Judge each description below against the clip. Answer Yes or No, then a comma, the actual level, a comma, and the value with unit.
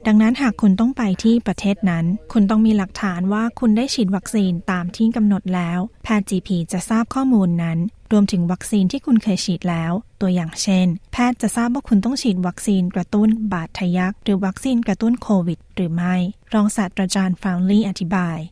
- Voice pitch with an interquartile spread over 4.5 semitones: No, average, 3.3 semitones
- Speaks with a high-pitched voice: Yes, high, 200 Hz